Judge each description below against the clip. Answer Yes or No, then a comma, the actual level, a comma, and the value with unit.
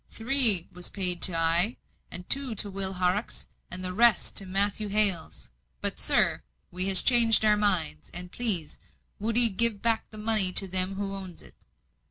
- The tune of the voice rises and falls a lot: No, average, 3.3 semitones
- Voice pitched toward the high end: Yes, high, 195 Hz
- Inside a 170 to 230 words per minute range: Yes, average, 175 wpm